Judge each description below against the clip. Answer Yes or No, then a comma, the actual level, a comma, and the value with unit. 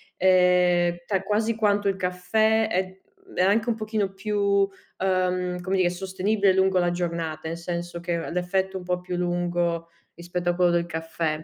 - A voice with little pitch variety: Yes, narrow, 1.8 semitones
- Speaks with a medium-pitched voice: Yes, medium, 180 Hz